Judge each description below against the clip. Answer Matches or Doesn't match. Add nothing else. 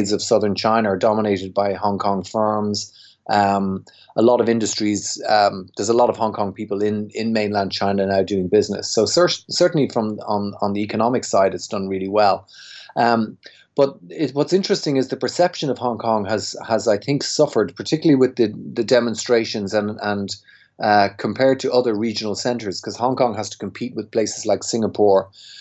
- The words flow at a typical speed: Matches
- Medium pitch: Doesn't match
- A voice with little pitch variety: Doesn't match